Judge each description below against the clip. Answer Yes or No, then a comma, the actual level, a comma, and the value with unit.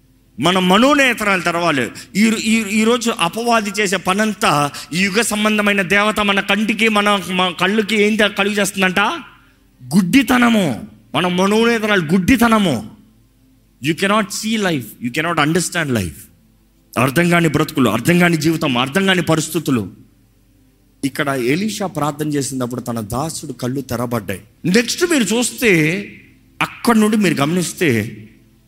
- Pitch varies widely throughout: Yes, wide, 8.3 semitones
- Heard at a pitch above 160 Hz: Yes, medium, 175 Hz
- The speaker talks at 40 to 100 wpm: No, average, 115 wpm